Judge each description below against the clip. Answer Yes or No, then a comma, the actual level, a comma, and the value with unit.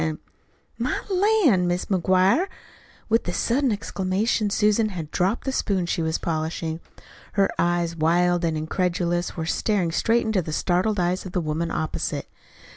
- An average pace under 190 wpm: Yes, average, 160 wpm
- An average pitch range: Yes, average, 3.5 semitones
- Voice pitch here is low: No, medium, 180 Hz